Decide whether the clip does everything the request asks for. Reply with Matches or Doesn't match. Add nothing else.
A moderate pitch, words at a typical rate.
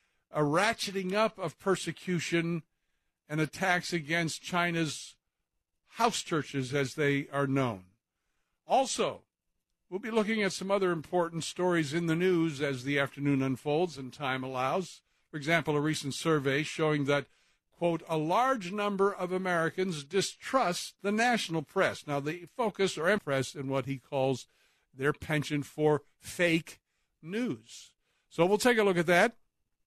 Matches